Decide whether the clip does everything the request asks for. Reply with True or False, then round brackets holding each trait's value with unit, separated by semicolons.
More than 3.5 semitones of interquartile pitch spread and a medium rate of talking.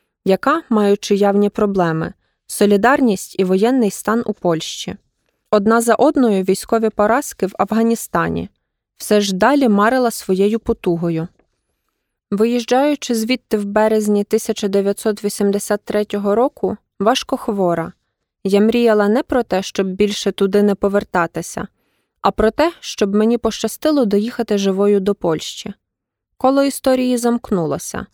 False (2.6 semitones; 115 wpm)